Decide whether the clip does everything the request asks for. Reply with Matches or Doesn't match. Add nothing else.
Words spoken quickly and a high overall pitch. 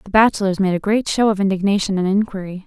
Matches